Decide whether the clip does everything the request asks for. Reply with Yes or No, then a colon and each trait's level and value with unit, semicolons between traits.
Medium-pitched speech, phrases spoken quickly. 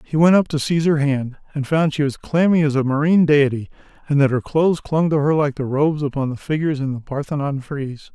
Yes: medium, 145 Hz; fast, 245 wpm